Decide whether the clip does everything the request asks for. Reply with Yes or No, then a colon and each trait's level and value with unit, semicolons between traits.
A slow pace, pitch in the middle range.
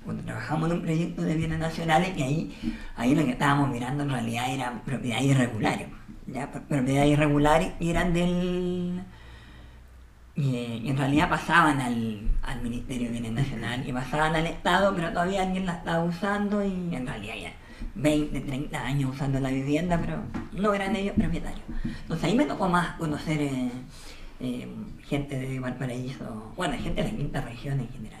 No: average, 170 wpm; medium, 145 Hz